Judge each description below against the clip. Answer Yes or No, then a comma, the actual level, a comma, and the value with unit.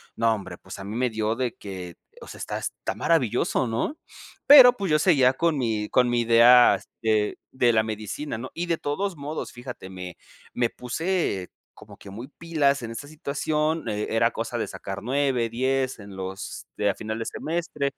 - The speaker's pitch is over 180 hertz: No, low, 120 Hz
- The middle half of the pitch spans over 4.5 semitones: Yes, average, 5.3 semitones